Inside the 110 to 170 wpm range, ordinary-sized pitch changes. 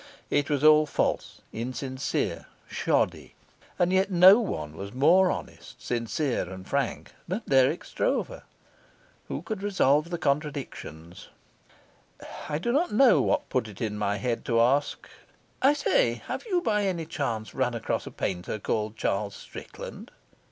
No: average, 145 wpm; wide, 8.6 semitones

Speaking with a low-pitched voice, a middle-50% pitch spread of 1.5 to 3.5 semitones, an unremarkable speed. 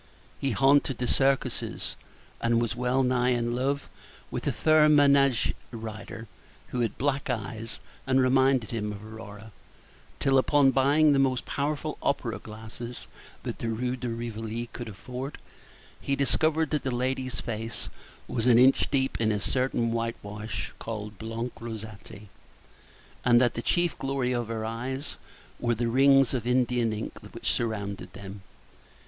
Yes: low, 120 Hz; average, 3.0 semitones; average, 150 wpm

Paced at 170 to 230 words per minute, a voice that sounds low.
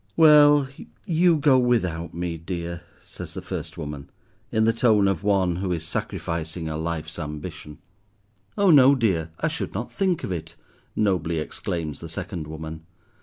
No: average, 160 wpm; very low, 90 Hz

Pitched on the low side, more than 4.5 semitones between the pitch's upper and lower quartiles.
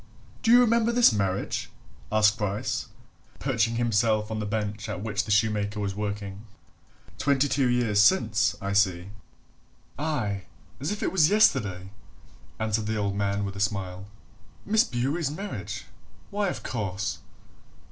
Yes: low, 110 Hz; average, 5.0 semitones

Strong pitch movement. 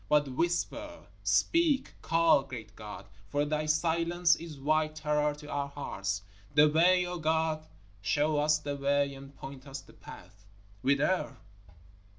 No: average, 2.9 semitones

